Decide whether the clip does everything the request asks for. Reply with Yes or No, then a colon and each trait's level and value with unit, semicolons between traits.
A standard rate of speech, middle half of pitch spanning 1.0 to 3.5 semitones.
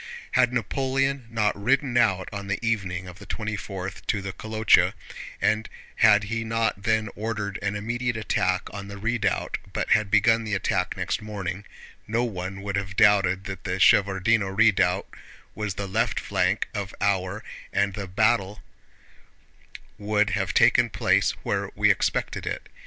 Yes: average, 160 wpm; narrow, 2.4 semitones